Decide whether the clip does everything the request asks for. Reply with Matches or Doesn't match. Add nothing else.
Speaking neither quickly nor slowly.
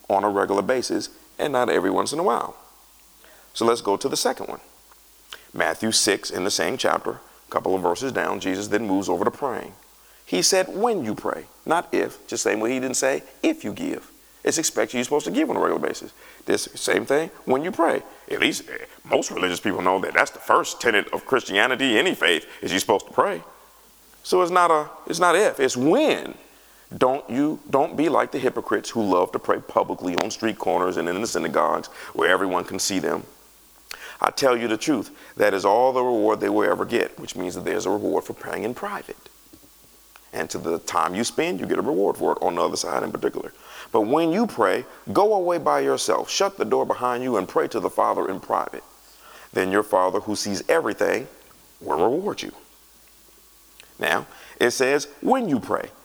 Doesn't match